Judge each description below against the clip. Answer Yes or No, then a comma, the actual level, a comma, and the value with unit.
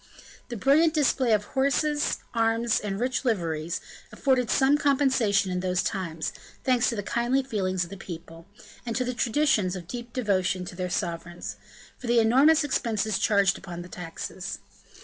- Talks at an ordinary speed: Yes, average, 165 wpm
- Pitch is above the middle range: Yes, high, 220 Hz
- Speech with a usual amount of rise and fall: No, wide, 5.9 semitones